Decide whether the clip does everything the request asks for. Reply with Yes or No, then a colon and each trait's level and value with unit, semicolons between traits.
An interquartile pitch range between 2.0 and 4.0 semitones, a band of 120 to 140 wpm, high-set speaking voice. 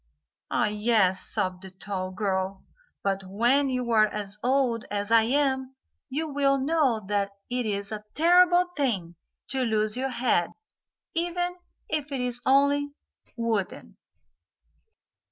No: wide, 5.4 semitones; slow, 135 wpm; high, 235 Hz